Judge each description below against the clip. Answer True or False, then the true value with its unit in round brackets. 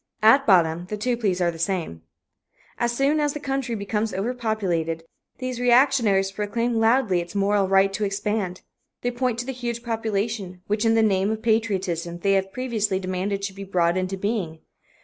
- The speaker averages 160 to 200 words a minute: True (180 wpm)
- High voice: True (205 Hz)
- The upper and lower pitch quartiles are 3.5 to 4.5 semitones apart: True (3.9 semitones)